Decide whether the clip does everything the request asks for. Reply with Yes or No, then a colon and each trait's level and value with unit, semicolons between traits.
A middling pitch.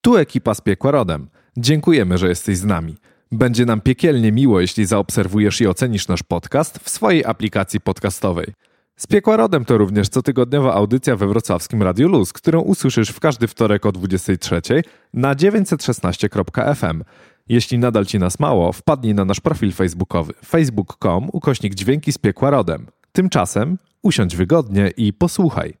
No: low, 110 Hz